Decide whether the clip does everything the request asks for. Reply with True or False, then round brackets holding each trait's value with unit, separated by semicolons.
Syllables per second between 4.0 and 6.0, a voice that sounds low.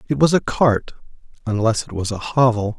True (5.3 syllables/s; 120 Hz)